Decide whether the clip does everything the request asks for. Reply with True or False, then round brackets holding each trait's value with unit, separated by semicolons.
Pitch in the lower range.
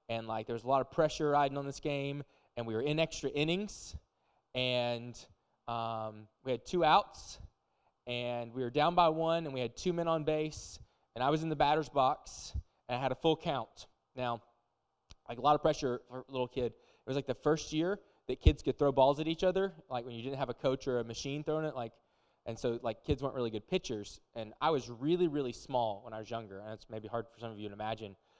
True (125 Hz)